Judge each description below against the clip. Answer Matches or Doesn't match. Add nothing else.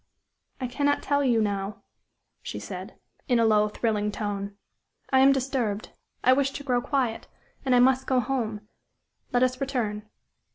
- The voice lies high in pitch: Matches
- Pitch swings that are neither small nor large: Matches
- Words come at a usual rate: Matches